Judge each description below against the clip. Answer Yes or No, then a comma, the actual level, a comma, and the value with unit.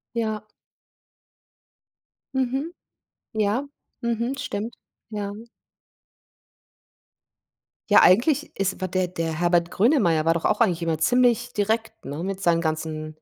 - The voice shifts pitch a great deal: Yes, wide, 5.7 semitones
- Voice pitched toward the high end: Yes, high, 200 Hz